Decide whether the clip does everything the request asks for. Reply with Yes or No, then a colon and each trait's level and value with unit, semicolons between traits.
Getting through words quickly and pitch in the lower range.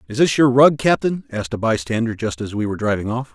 Yes: fast, 250 wpm; low, 120 Hz